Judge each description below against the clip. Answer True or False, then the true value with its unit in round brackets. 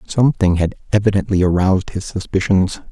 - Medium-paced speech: False (125 wpm)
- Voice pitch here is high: False (95 Hz)